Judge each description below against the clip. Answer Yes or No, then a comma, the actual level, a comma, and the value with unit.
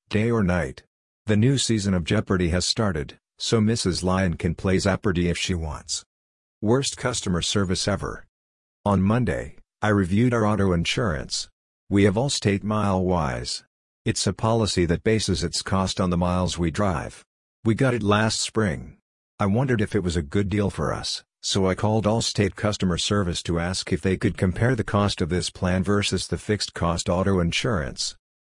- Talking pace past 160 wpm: Yes, average, 175 wpm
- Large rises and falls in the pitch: No, average, 3.1 semitones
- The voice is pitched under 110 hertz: Yes, very low, 95 Hz